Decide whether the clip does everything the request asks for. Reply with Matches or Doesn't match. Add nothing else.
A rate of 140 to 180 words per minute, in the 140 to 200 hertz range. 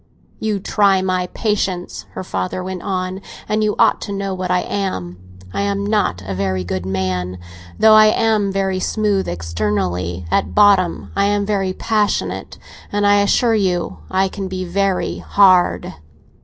Matches